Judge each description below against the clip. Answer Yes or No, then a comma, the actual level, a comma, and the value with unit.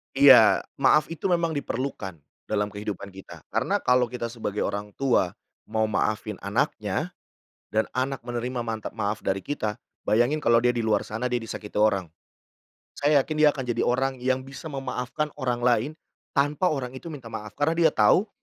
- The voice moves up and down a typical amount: Yes, average, 4.4 semitones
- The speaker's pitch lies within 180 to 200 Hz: No, low, 120 Hz